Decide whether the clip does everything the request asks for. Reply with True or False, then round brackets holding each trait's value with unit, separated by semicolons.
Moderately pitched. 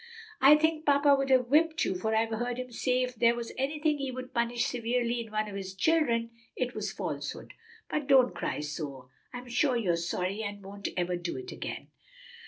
False (240 Hz)